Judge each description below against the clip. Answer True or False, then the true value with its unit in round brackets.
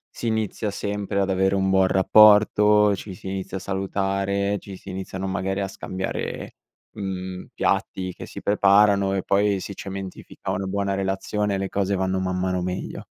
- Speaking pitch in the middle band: False (95 Hz)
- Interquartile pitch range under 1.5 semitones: True (1.1 semitones)